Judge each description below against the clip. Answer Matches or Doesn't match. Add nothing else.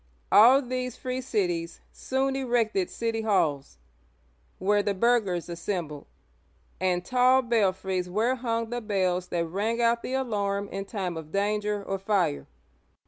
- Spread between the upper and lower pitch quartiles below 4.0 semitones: Doesn't match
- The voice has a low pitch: Doesn't match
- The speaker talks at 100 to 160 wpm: Matches